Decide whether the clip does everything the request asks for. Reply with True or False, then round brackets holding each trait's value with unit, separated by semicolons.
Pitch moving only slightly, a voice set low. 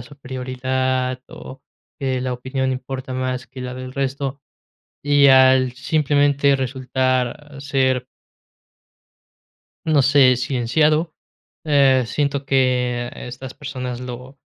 True (1.6 semitones; 130 Hz)